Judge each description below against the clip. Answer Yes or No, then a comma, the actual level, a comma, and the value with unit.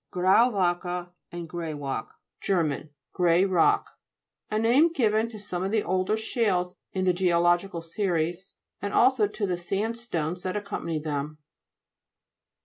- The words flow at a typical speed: No, slow, 130 wpm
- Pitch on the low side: No, medium, 185 Hz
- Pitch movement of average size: Yes, average, 3.4 semitones